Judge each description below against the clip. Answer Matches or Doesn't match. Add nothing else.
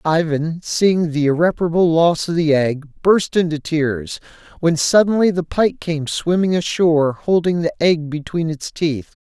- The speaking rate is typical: Matches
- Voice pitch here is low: Doesn't match